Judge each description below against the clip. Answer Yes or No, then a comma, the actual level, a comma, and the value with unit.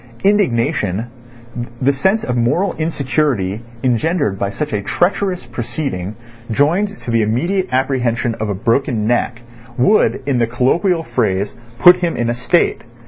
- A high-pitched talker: No, low, 125 Hz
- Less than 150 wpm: Yes, average, 140 wpm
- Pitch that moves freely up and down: Yes, wide, 6.3 semitones